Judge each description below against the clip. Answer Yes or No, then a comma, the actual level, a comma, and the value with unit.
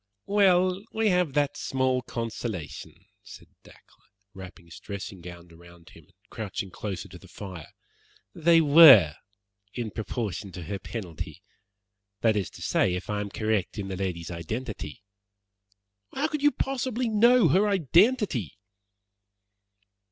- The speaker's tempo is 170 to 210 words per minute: No, slow, 135 wpm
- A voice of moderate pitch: No, low, 110 Hz